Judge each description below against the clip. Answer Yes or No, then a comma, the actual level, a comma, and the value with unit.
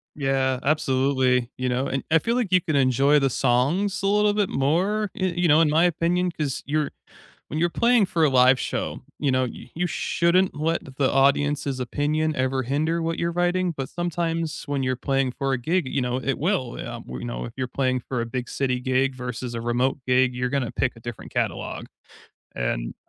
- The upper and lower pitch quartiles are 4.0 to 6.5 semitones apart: Yes, average, 4.5 semitones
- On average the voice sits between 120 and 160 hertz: Yes, medium, 140 Hz